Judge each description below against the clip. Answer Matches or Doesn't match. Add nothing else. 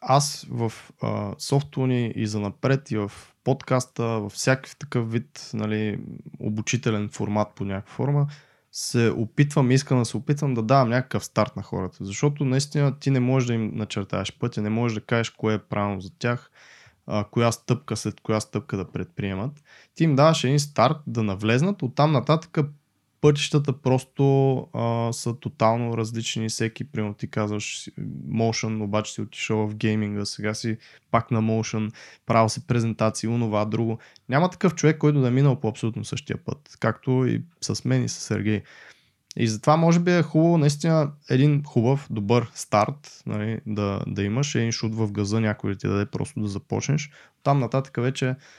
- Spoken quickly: Matches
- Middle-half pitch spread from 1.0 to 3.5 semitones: Doesn't match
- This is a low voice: Matches